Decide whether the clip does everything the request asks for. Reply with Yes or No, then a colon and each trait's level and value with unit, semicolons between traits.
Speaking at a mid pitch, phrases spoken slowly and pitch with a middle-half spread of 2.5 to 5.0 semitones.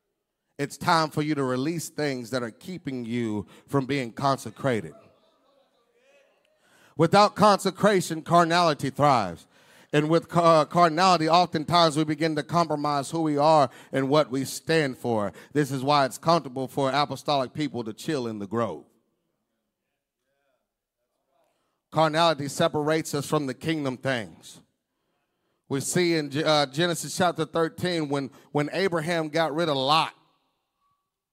Yes: medium, 150 Hz; slow, 130 wpm; average, 3.4 semitones